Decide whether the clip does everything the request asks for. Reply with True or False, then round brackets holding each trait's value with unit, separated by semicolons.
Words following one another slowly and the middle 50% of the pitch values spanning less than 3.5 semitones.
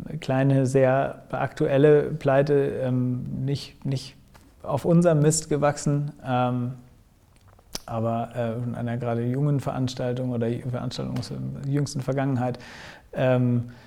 True (95 wpm; 2.5 semitones)